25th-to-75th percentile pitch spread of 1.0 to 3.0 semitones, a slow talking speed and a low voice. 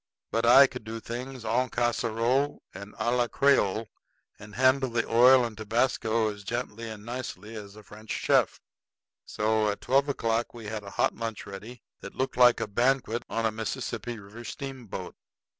No: narrow, 2.5 semitones; average, 175 wpm; low, 115 Hz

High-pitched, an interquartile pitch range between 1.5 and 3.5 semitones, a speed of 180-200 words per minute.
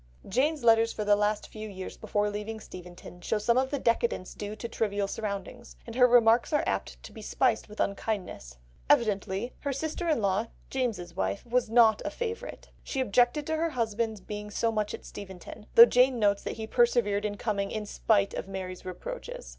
Yes: high, 220 Hz; average, 3.1 semitones; average, 195 wpm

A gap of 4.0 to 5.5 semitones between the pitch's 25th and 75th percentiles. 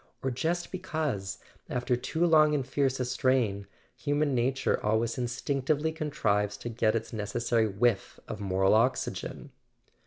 Yes: average, 5.0 semitones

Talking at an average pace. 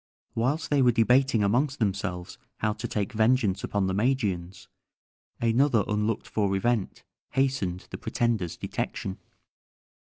No: slow, 125 wpm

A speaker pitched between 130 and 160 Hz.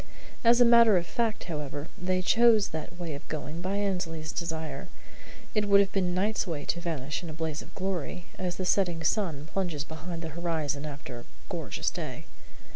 No: medium, 175 Hz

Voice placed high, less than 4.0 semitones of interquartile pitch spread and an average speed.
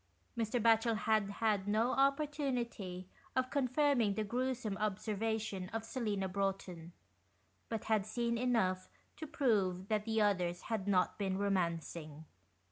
No: high, 215 Hz; average, 3.6 semitones; slow, 130 wpm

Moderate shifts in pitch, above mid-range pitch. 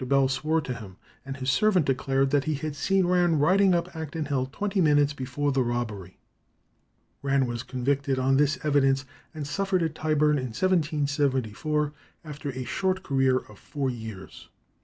No: average, 3.1 semitones; medium, 140 Hz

